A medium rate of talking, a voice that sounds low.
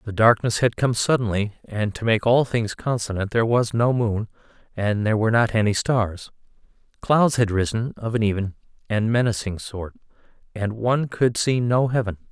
Yes: average, 175 wpm; low, 110 Hz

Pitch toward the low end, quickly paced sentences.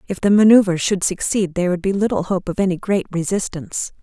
No: high, 190 Hz; fast, 210 wpm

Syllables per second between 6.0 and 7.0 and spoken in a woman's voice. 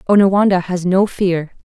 No: 5.0 syllables/s; female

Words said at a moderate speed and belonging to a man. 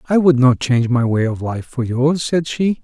No: fast, 255 wpm; male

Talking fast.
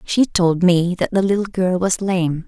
Yes: fast, 220 wpm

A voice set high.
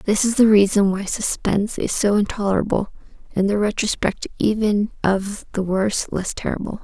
Yes: high, 205 Hz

